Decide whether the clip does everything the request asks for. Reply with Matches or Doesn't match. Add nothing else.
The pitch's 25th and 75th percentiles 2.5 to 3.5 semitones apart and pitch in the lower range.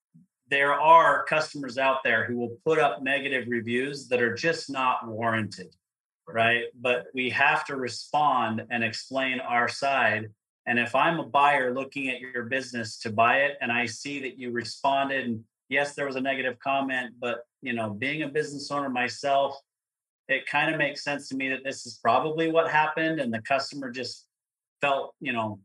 Matches